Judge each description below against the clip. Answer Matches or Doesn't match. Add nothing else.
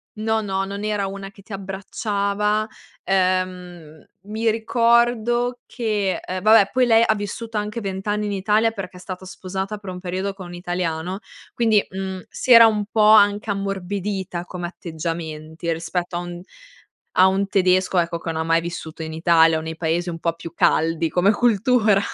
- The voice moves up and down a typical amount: Matches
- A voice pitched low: Doesn't match